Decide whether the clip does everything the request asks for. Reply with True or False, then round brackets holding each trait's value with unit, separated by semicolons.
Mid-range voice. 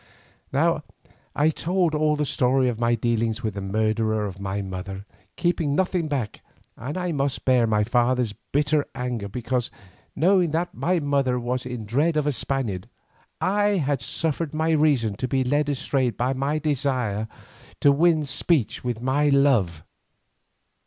False (130 Hz)